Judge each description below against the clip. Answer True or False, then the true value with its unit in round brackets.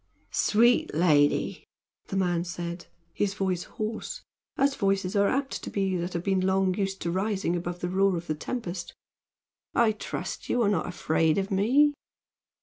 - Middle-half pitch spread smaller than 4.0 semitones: True (2.8 semitones)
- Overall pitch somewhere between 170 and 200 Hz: True (190 Hz)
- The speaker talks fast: False (165 wpm)